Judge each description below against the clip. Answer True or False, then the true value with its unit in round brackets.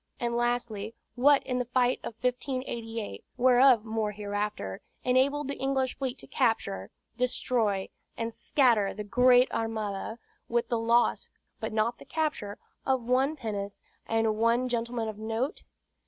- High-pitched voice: True (235 Hz)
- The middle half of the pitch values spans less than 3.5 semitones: True (2.7 semitones)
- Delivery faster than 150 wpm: False (140 wpm)